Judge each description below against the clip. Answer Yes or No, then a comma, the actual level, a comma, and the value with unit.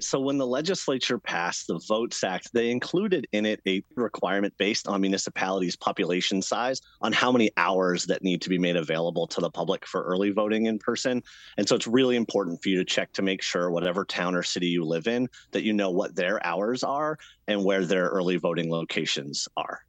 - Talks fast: Yes, fast, 210 wpm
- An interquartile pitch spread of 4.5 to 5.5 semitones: No, average, 4.0 semitones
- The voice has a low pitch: Yes, low, 100 Hz